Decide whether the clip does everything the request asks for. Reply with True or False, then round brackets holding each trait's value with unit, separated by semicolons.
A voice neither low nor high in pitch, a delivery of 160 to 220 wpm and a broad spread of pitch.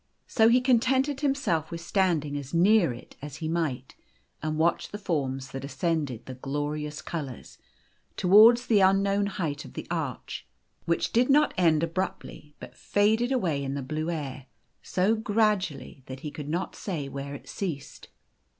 True (165 Hz; 170 wpm; 6.2 semitones)